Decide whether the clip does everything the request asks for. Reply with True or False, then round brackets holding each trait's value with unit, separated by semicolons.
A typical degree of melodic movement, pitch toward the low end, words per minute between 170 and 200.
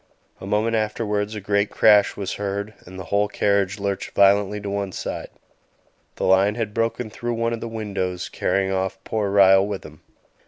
False (1.6 semitones; 100 Hz; 185 wpm)